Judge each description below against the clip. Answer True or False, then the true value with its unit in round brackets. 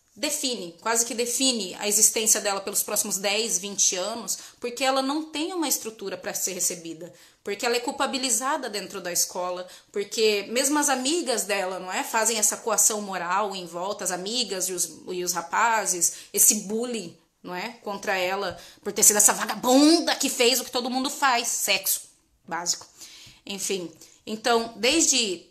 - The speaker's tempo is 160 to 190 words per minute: True (165 wpm)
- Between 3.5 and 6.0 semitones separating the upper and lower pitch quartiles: True (4.6 semitones)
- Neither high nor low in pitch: False (210 Hz)